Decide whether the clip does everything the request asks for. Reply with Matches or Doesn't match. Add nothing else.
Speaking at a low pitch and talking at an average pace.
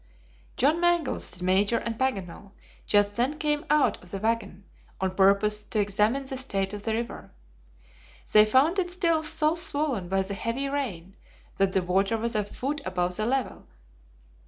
Doesn't match